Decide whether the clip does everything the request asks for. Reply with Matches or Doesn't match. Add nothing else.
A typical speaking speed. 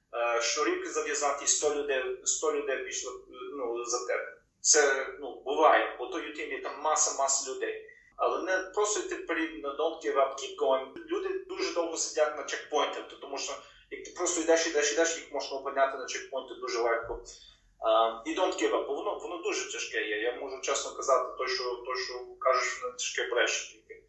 Doesn't match